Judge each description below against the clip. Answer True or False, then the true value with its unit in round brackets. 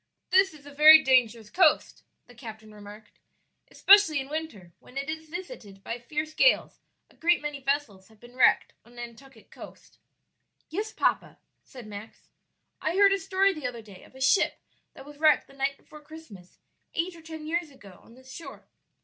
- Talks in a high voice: True (275 Hz)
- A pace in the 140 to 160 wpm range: False (185 wpm)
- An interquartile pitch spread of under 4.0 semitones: False (5.6 semitones)